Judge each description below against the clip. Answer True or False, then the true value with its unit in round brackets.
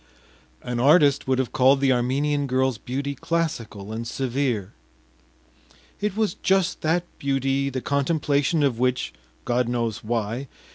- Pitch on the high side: False (135 Hz)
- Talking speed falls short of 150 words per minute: True (135 wpm)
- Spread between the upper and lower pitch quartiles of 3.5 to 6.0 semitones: False (2.8 semitones)